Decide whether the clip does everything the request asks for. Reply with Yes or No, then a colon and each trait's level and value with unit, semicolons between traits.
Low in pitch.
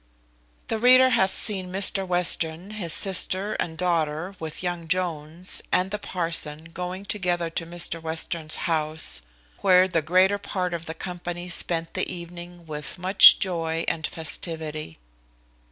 No: medium, 175 Hz